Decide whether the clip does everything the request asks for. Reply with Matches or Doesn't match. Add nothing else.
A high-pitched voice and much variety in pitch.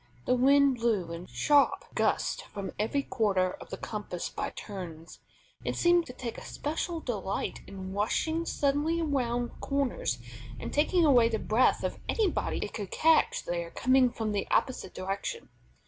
Matches